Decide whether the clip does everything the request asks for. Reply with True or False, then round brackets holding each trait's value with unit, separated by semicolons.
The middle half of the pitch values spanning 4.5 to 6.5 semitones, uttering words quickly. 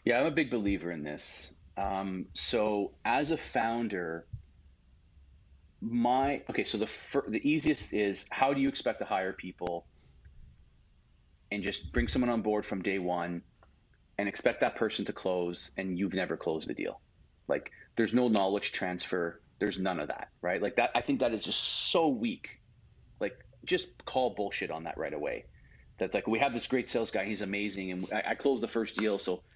False (4.9 semitones; 185 wpm)